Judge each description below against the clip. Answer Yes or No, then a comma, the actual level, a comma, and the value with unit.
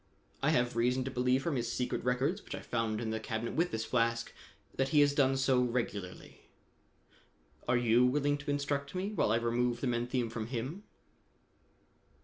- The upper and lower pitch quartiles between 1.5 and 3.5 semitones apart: Yes, average, 3.0 semitones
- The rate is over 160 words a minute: Yes, average, 180 wpm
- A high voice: No, low, 125 Hz